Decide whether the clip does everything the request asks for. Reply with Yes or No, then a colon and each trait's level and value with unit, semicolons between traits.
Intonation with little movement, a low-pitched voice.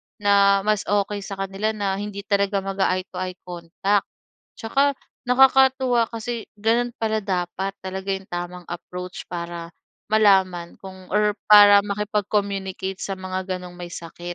No: narrow, 2.2 semitones; high, 195 Hz